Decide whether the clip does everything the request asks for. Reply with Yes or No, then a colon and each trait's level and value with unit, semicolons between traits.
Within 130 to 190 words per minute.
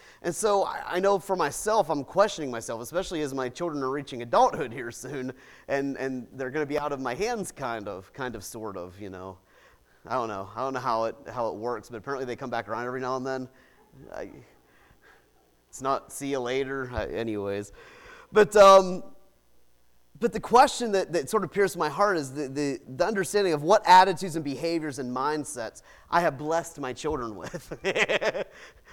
No: average, 200 wpm